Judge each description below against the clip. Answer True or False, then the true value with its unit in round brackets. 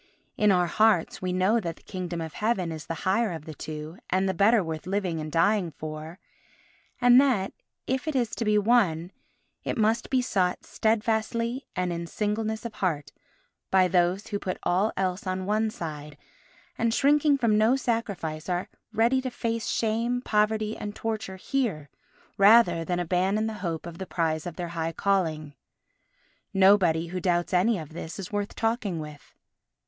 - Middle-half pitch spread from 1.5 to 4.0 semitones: False (4.6 semitones)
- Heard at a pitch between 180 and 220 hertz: True (190 Hz)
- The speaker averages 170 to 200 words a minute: True (175 wpm)